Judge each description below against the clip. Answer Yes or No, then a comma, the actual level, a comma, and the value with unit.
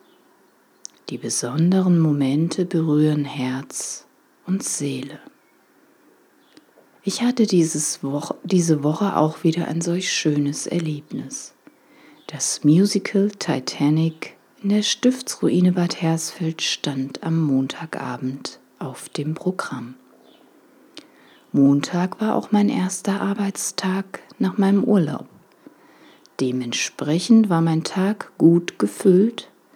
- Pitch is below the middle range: No, medium, 165 Hz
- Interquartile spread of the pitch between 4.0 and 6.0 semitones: Yes, average, 5.0 semitones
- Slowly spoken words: Yes, slow, 95 wpm